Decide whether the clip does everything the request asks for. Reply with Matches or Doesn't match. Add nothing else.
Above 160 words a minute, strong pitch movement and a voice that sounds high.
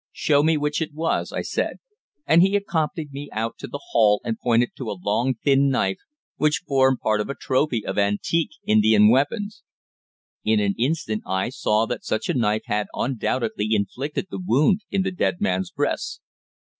Doesn't match